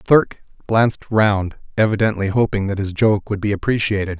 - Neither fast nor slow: Yes, average, 170 wpm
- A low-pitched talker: Yes, low, 105 Hz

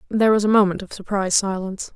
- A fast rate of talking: Yes, fast, 215 wpm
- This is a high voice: Yes, high, 200 Hz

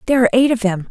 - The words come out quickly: Yes, fast, 330 wpm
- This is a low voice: No, high, 230 Hz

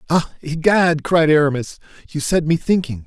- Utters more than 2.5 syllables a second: Yes, 4.8 syllables/s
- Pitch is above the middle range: No, medium, 160 Hz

